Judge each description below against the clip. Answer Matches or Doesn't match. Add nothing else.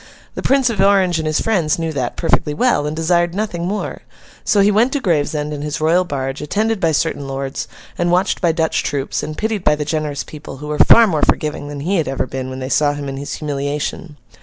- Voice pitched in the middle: Matches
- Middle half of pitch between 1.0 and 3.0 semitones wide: Doesn't match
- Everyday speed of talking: Doesn't match